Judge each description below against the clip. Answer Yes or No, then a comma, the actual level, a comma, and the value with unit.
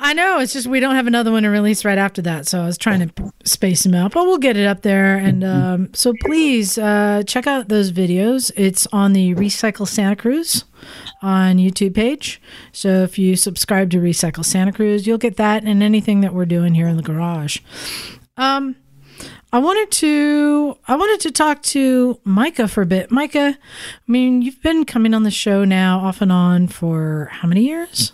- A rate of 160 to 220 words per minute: Yes, fast, 205 wpm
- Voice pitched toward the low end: No, high, 210 Hz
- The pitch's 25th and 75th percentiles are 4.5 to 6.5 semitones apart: Yes, average, 5.3 semitones